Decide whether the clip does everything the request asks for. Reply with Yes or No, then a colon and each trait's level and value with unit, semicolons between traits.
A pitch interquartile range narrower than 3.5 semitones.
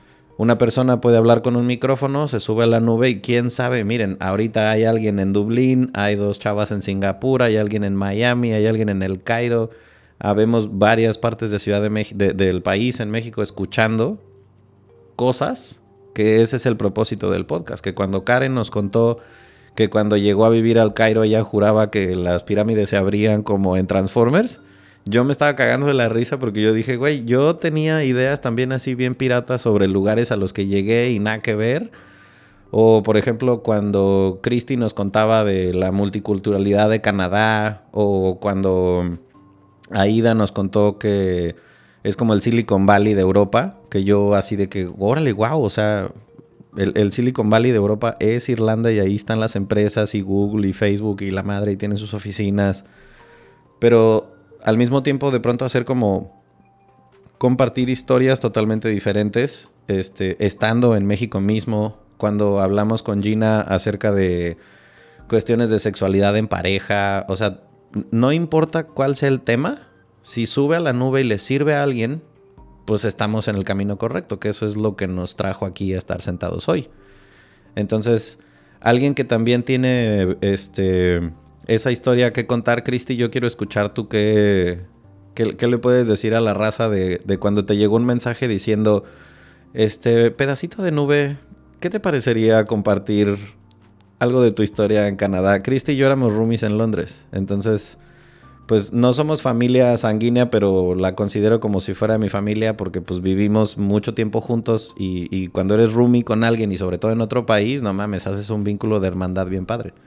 Yes: average, 3.1 semitones